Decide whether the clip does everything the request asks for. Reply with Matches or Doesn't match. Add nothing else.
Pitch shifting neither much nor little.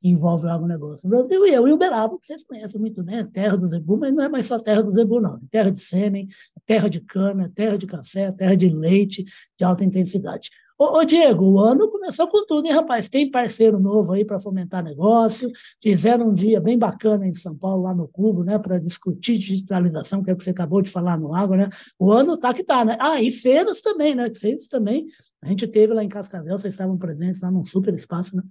Matches